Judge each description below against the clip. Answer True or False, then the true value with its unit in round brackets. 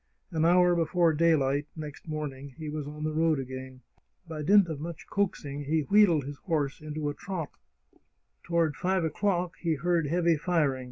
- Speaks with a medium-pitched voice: True (155 Hz)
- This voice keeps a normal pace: True (170 wpm)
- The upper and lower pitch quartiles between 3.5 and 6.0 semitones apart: False (2.8 semitones)